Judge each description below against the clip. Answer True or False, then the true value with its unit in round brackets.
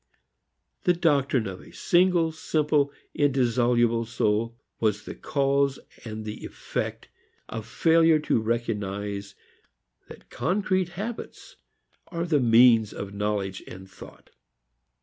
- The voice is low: True (120 Hz)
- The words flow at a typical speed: False (115 wpm)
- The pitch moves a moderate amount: False (6.8 semitones)